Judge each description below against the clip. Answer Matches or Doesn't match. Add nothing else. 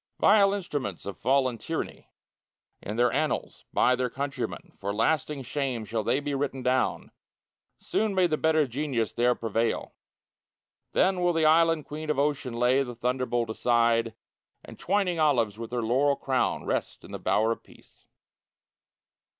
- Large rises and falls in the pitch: Doesn't match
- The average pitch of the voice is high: Doesn't match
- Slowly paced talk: Doesn't match